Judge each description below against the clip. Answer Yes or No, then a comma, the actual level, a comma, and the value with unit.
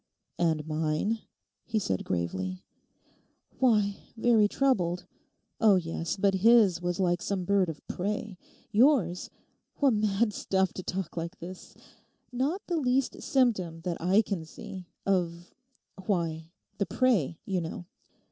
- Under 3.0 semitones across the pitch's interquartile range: No, average, 4.5 semitones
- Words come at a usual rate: No, slow, 115 wpm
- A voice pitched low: No, high, 190 Hz